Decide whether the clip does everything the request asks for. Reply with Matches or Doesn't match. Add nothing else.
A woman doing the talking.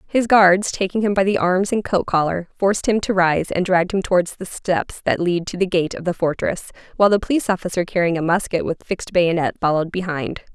Matches